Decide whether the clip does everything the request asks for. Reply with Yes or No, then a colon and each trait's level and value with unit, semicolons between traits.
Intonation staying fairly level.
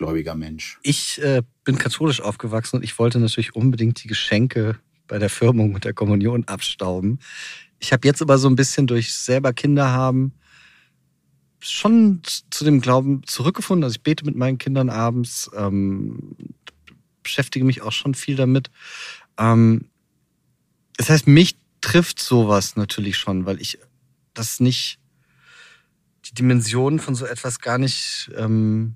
No: average, 3.6 semitones